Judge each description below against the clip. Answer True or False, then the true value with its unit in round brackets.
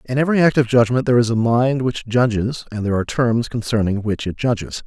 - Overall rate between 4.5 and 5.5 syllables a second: False (6.5 syllables/s)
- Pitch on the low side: True (120 Hz)